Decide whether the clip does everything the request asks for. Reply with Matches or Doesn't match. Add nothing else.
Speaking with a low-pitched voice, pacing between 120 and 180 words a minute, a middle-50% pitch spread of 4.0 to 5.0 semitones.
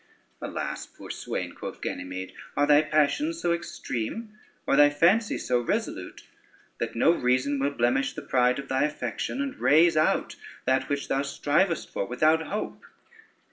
Doesn't match